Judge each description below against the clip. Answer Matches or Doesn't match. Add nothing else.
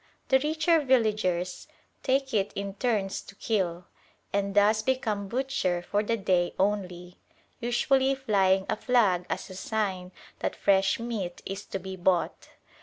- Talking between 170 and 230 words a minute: Doesn't match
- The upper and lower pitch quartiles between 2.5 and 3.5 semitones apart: Doesn't match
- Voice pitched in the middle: Doesn't match